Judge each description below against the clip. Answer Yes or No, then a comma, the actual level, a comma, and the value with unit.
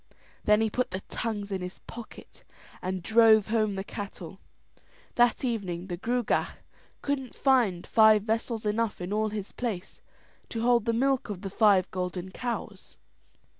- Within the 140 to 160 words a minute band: Yes, average, 150 wpm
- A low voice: No, high, 215 Hz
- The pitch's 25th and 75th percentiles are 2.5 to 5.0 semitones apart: Yes, average, 3.5 semitones